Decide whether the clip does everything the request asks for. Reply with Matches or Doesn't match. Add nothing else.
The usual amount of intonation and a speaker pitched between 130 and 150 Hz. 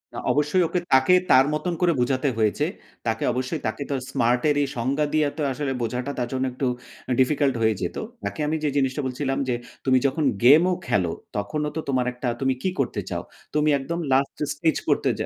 Matches